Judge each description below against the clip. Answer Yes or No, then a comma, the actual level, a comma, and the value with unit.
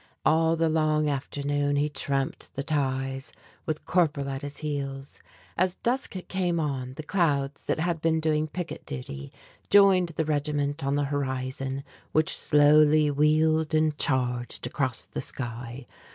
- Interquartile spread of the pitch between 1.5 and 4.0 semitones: Yes, narrow, 2.4 semitones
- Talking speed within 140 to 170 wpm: Yes, average, 145 wpm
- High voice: No, medium, 145 Hz